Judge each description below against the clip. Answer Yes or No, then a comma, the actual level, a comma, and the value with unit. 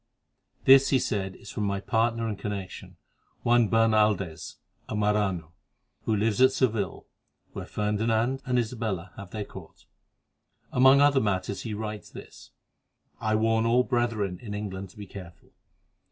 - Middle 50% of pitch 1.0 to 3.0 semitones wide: Yes, narrow, 2.6 semitones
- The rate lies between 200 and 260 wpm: No, average, 145 wpm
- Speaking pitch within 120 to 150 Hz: No, low, 110 Hz